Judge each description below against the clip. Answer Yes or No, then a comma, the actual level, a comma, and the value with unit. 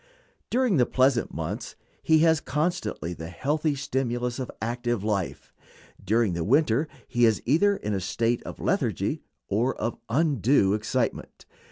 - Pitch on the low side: Yes, low, 120 Hz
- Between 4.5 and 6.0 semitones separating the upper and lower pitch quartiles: Yes, average, 5.3 semitones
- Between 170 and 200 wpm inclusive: No, average, 145 wpm